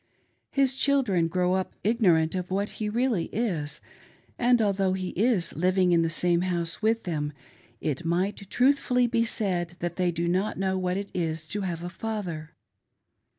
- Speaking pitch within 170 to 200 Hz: Yes, medium, 185 Hz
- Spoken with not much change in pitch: No, average, 4.0 semitones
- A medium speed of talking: Yes, average, 170 wpm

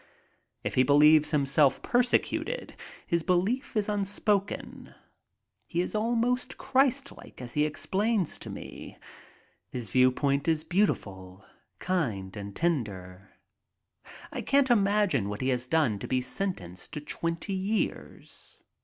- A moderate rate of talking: No, slow, 120 wpm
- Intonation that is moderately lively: No, wide, 8.3 semitones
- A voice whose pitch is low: No, medium, 160 Hz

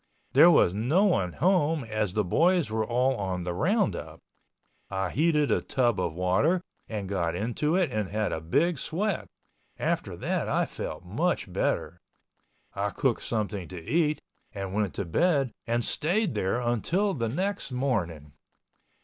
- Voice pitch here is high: No, low, 120 Hz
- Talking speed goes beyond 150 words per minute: Yes, average, 160 wpm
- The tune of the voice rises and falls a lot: Yes, wide, 8.4 semitones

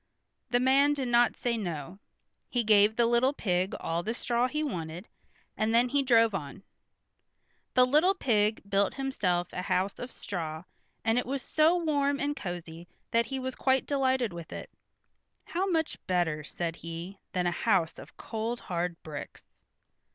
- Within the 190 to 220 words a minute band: No, average, 165 wpm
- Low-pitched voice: No, high, 225 Hz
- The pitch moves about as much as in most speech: No, wide, 6.7 semitones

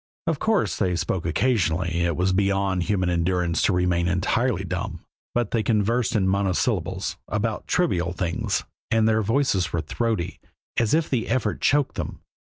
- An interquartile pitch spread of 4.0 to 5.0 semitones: Yes, average, 4.5 semitones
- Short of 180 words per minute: Yes, average, 160 wpm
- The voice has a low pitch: Yes, low, 100 Hz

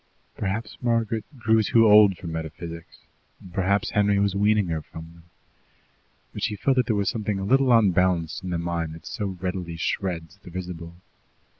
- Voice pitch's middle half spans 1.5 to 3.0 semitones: No, average, 4.0 semitones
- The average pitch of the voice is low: Yes, very low, 95 Hz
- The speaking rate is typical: Yes, average, 170 wpm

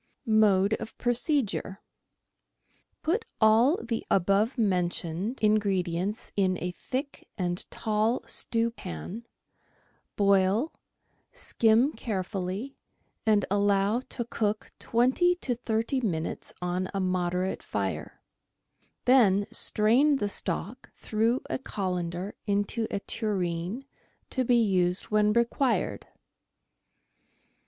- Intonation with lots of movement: No, average, 4.0 semitones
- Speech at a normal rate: No, slow, 100 wpm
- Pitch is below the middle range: No, high, 210 Hz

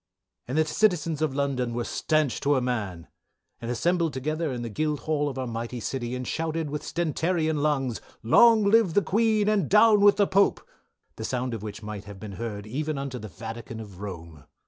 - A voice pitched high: No, low, 135 Hz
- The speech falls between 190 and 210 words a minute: Yes, average, 195 wpm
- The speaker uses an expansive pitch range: Yes, wide, 6.0 semitones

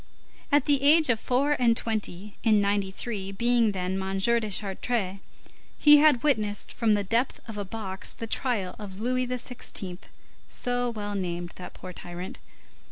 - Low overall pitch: No, high, 215 Hz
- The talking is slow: No, average, 160 wpm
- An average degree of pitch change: Yes, average, 4.3 semitones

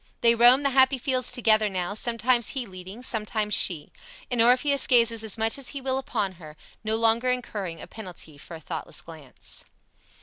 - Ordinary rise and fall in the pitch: Yes, average, 4.8 semitones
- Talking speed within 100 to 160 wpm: No, average, 180 wpm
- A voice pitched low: No, high, 225 Hz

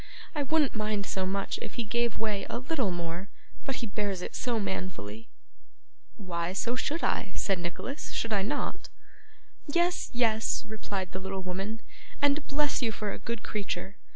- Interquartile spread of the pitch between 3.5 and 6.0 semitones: Yes, average, 4.4 semitones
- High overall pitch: Yes, high, 210 Hz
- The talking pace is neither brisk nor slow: Yes, average, 170 wpm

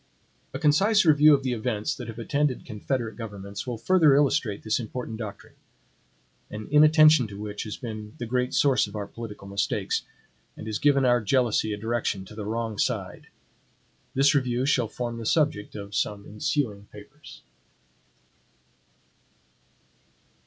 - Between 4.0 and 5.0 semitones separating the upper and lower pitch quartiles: Yes, average, 4.5 semitones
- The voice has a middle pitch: No, low, 115 Hz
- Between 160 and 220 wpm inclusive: No, average, 150 wpm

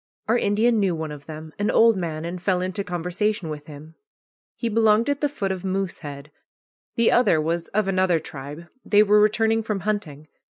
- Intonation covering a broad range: No, average, 5.0 semitones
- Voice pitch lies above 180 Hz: Yes, high, 190 Hz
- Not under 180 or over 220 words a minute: Yes, average, 190 wpm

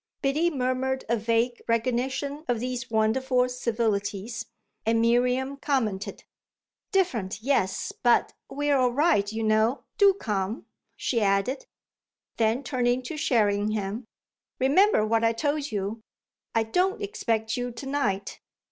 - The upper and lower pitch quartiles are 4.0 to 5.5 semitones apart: No, average, 3.5 semitones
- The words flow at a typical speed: No, slow, 125 wpm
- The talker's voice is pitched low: No, high, 240 Hz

